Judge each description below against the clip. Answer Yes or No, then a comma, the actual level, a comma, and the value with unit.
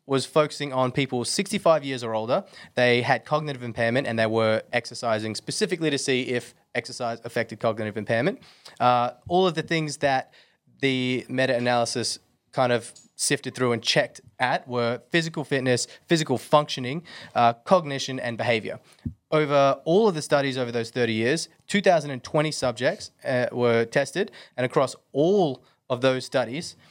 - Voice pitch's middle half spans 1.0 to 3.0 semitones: No, average, 3.9 semitones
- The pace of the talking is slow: No, average, 155 wpm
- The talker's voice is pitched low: Yes, low, 130 Hz